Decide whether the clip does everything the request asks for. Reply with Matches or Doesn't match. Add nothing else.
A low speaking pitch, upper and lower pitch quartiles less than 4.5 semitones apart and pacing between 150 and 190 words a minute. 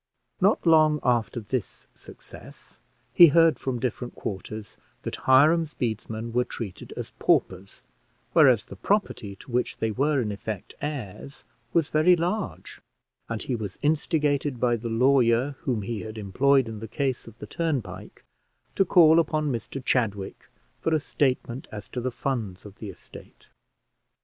Doesn't match